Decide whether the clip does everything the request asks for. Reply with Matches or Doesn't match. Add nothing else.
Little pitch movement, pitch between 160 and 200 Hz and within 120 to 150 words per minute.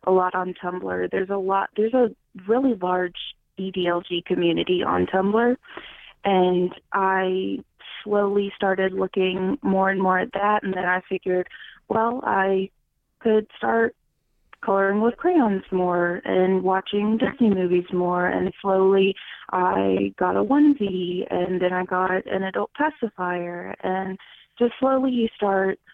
Matches